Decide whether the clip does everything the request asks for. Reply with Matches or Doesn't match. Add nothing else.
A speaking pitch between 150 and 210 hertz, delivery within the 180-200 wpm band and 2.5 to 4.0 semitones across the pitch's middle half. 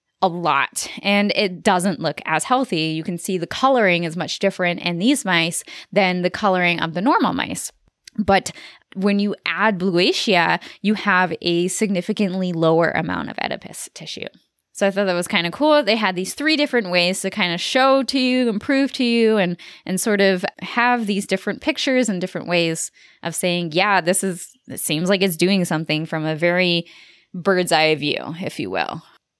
Matches